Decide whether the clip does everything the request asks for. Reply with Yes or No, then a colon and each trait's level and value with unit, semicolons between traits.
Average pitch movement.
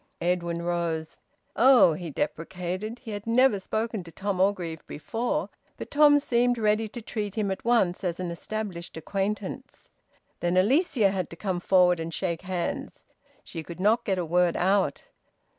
Yes: average, 4.1 semitones